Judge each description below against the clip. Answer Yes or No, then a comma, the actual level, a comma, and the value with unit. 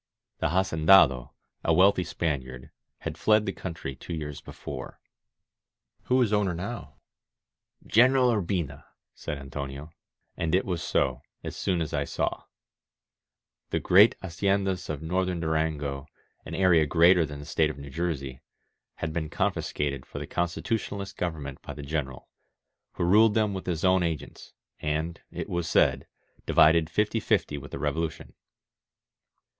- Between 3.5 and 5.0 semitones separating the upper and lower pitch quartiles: Yes, average, 4.4 semitones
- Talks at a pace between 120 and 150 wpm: Yes, average, 145 wpm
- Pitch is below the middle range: Yes, very low, 80 Hz